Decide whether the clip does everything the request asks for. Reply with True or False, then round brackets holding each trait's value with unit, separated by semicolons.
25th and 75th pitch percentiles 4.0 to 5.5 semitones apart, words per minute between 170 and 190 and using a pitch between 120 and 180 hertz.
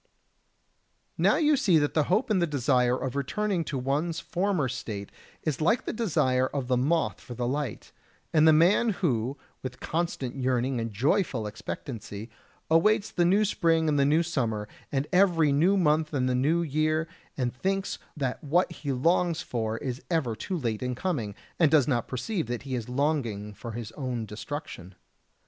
True (5.2 semitones; 180 wpm; 140 Hz)